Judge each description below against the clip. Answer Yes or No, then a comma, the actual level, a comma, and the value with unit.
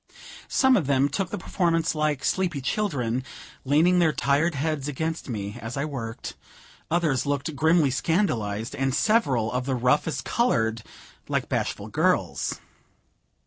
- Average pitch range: Yes, average, 4.6 semitones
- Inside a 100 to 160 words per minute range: Yes, average, 140 wpm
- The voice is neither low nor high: Yes, medium, 145 Hz